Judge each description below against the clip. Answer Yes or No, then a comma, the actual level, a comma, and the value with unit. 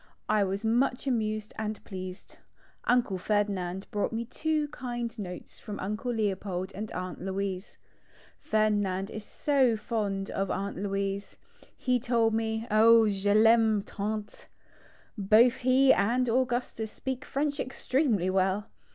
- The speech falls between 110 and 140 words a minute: Yes, slow, 135 wpm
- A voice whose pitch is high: Yes, high, 215 Hz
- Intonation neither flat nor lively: Yes, average, 3.3 semitones